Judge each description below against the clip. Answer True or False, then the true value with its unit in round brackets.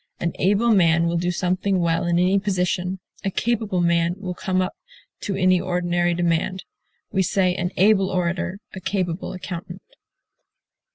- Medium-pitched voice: True (180 Hz)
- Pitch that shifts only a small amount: True (1.6 semitones)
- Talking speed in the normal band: True (155 wpm)